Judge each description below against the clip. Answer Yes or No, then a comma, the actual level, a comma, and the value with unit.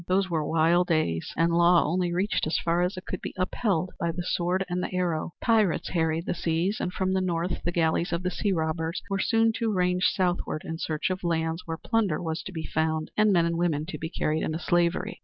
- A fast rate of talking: Yes, fast, 230 wpm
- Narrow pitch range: Yes, narrow, 2.2 semitones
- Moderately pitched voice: Yes, medium, 175 Hz